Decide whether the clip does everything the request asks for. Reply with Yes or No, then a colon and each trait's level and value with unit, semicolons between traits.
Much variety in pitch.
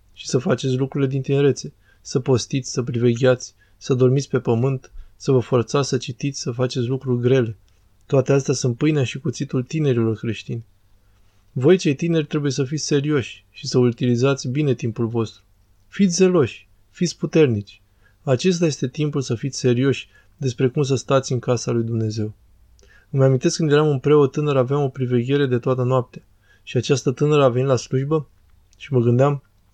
No: average, 4.0 semitones